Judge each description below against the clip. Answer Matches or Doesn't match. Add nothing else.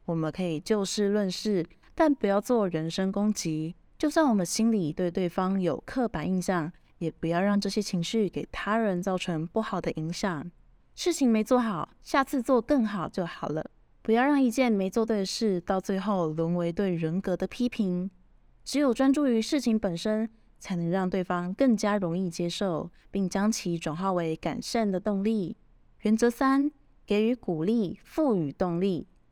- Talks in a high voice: Matches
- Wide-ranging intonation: Doesn't match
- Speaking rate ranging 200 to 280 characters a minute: Matches